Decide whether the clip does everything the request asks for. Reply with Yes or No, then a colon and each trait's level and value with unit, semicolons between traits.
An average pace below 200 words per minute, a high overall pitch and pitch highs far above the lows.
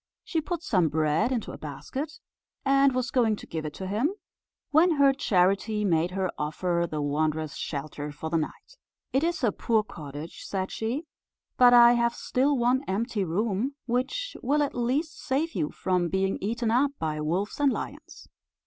Yes: average, 175 wpm; high, 220 Hz; wide, 8.0 semitones